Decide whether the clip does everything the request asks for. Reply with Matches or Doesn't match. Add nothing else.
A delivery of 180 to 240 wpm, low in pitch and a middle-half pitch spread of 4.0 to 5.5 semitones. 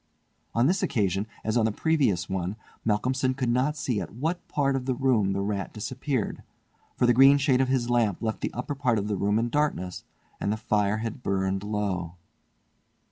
Matches